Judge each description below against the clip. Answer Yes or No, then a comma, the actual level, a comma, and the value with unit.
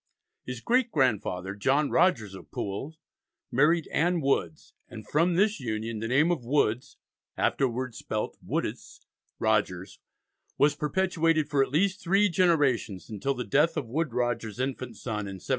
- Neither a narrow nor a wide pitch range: No, wide, 6.3 semitones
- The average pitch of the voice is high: No, low, 135 Hz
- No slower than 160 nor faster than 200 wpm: No, average, 150 wpm